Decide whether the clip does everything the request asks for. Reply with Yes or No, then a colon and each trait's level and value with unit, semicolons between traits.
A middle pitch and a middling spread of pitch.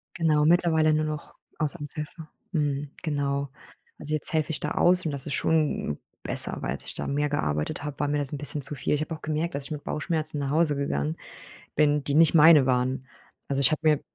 No: medium, 150 Hz; narrow, 1.8 semitones